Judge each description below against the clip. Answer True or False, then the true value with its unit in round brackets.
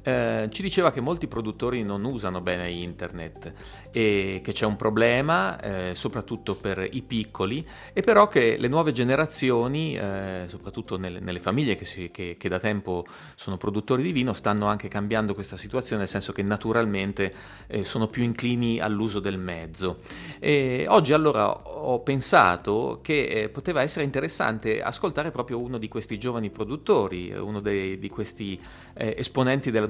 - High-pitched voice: False (110 Hz)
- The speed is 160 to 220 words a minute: True (165 wpm)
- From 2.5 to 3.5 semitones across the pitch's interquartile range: False (4.3 semitones)